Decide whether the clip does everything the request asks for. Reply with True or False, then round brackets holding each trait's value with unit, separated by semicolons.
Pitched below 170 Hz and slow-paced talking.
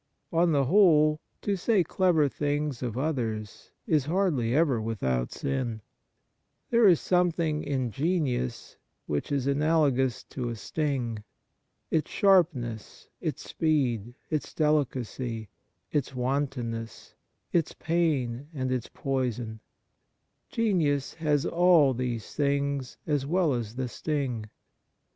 True (140 Hz; 115 wpm)